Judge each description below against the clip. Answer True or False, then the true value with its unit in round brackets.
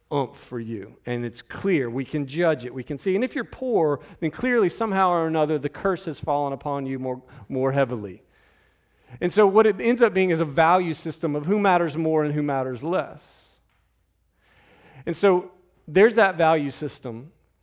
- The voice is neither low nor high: True (160 Hz)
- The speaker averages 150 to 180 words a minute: False (190 wpm)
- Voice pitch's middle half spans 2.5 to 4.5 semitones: False (5.5 semitones)